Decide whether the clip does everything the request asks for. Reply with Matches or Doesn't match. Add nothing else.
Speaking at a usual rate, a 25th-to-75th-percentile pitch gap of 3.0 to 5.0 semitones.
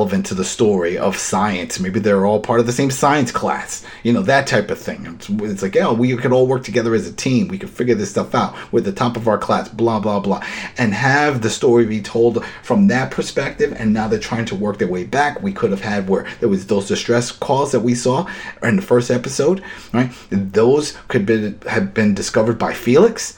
Doesn't match